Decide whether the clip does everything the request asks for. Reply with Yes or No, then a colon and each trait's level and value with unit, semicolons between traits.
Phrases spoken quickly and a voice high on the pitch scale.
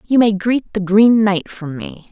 Yes: fast, 225 wpm; high, 205 Hz